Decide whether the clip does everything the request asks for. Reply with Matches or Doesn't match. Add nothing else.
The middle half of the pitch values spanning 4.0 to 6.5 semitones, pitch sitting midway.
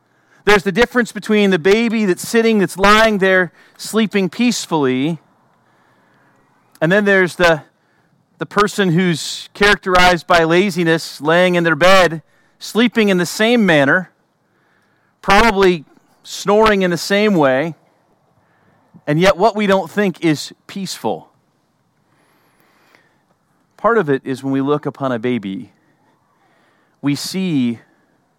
Matches